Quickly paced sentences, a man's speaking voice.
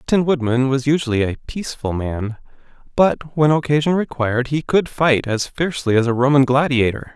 No: average, 175 wpm; male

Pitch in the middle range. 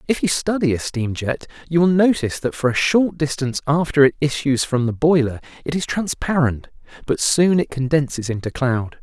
Yes: medium, 145 Hz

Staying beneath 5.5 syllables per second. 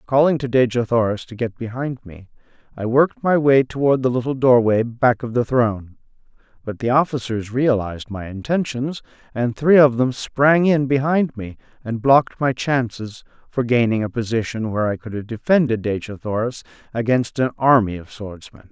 Yes: 5.1 syllables/s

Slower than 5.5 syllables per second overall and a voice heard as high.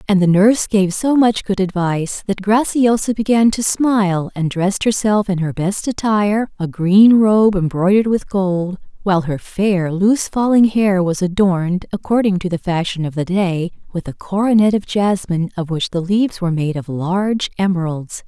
Yes: 5.0 syllables/s; high, 195 Hz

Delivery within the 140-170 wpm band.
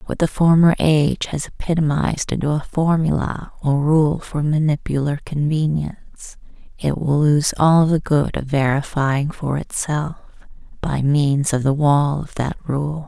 Yes: average, 145 wpm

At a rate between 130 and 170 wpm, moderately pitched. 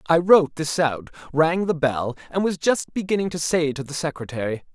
No: average, 200 wpm; medium, 155 Hz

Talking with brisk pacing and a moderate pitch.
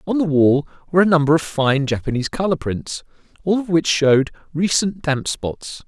No: average, 185 wpm; medium, 155 Hz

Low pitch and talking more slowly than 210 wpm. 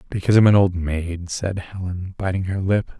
Yes: very low, 95 Hz; average, 200 wpm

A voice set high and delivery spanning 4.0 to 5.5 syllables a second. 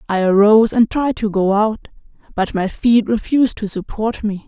Yes: high, 215 Hz; 5.0 syllables/s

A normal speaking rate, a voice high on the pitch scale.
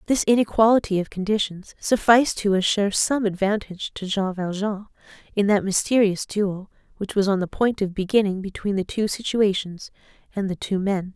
Yes: average, 165 wpm; high, 200 Hz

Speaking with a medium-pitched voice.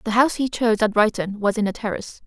No: high, 220 Hz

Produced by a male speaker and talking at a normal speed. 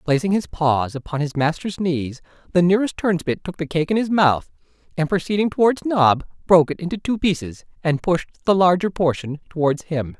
Yes: male; average, 190 wpm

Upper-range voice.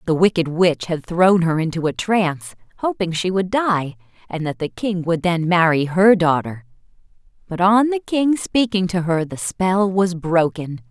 No: medium, 180 Hz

